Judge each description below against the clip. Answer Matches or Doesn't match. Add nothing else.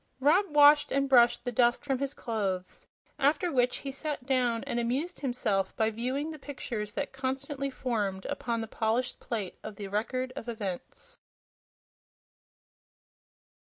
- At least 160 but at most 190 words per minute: Doesn't match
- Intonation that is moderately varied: Matches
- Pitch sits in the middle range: Doesn't match